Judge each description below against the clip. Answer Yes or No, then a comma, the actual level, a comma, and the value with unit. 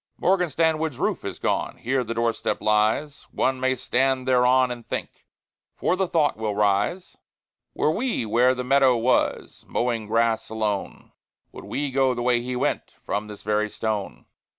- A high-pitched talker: No, low, 125 Hz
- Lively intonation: No, average, 3.4 semitones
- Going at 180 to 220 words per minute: No, average, 170 wpm